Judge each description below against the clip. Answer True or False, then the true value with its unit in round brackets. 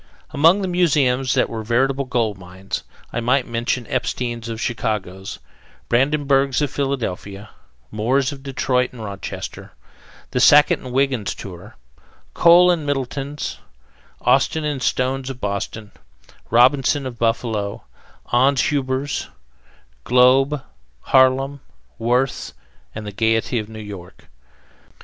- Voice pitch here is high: False (125 Hz)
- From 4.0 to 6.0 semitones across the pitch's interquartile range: False (3.6 semitones)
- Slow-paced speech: True (115 wpm)